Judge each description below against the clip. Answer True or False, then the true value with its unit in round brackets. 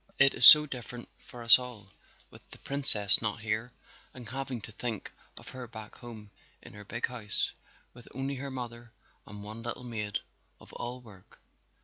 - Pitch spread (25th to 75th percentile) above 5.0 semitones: False (2.7 semitones)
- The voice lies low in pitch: True (120 Hz)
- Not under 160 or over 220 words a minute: True (175 wpm)